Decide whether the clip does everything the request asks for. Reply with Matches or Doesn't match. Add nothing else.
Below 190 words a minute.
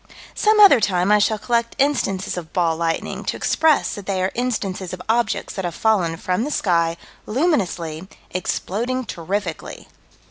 Matches